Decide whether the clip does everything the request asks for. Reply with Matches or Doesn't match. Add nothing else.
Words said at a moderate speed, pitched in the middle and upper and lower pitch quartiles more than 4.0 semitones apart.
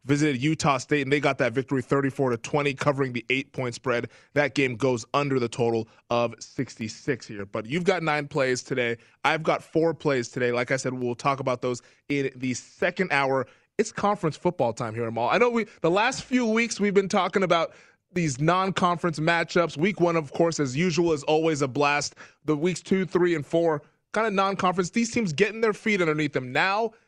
Doesn't match